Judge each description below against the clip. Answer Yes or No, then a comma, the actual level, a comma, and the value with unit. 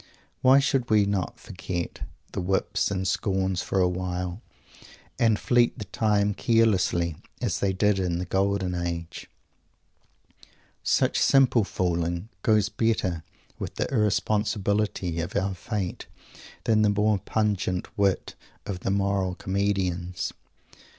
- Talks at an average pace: No, slow, 125 wpm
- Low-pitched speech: Yes, very low, 95 Hz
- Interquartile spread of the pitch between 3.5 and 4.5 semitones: No, average, 2.8 semitones